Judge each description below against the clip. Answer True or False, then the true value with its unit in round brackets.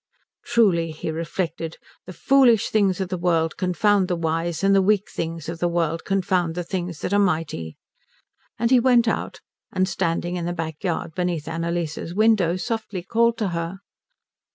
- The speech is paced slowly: False (175 wpm)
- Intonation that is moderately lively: True (3.2 semitones)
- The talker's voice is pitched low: False (175 Hz)